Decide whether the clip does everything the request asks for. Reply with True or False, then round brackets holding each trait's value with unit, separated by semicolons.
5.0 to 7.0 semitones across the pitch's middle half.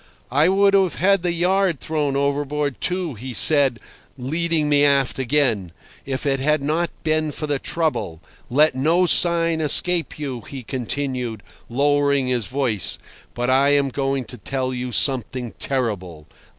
False (3.6 semitones)